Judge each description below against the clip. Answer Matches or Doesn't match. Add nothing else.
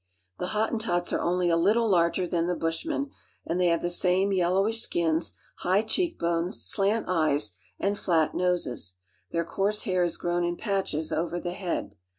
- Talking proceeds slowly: Doesn't match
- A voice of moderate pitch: Matches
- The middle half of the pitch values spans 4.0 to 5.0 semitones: Doesn't match